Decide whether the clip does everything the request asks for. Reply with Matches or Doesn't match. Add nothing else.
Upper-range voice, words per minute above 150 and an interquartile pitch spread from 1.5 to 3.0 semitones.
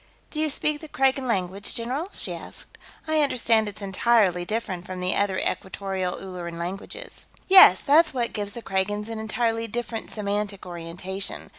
Doesn't match